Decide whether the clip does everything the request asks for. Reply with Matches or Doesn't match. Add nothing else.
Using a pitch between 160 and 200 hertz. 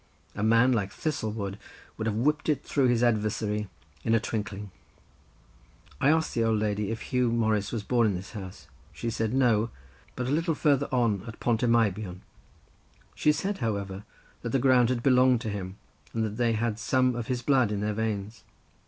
Doesn't match